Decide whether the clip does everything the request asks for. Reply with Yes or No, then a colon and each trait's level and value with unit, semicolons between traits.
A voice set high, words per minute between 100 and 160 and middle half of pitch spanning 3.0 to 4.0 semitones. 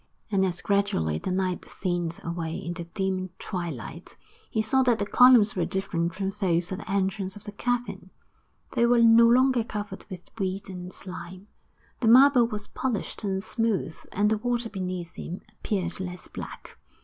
No: high, 195 Hz; average, 170 wpm; average, 3.6 semitones